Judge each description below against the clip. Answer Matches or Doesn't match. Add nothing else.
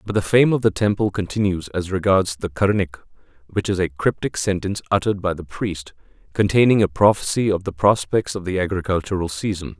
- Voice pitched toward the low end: Matches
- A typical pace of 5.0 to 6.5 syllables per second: Matches